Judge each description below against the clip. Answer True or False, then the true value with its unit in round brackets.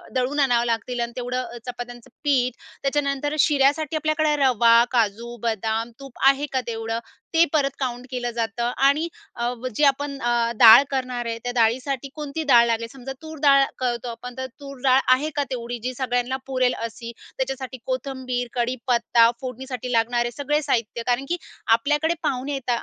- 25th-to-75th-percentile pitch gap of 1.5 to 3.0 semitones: True (2.5 semitones)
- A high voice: True (255 Hz)